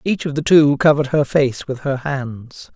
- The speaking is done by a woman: No, male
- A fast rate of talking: Yes, fast, 220 wpm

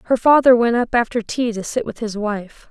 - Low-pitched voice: No, high, 230 Hz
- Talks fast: Yes, fast, 245 wpm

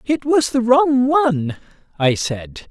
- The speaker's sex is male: Yes, male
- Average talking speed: Yes, average, 155 wpm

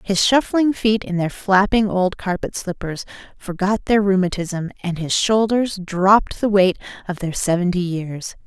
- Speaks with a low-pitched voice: No, high, 195 Hz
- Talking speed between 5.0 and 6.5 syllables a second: No, 4.4 syllables/s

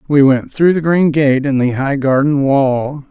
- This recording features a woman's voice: No, male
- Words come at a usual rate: No, fast, 215 wpm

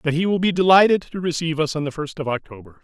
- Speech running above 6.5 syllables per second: Yes, 6.8 syllables/s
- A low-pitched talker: No, medium, 160 Hz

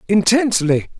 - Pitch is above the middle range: Yes, high, 195 Hz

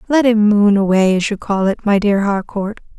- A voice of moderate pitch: No, high, 205 Hz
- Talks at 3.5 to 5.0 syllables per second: Yes, 4.9 syllables/s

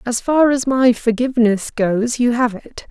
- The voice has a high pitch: Yes, high, 240 Hz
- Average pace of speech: Yes, average, 185 wpm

